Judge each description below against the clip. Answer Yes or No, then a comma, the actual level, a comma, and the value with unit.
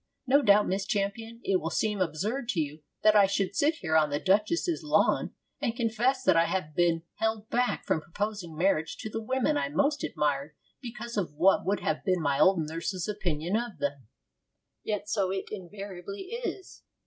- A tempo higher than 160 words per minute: Yes, average, 185 wpm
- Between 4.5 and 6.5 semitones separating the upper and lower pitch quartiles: Yes, average, 5.2 semitones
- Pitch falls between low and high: No, high, 195 Hz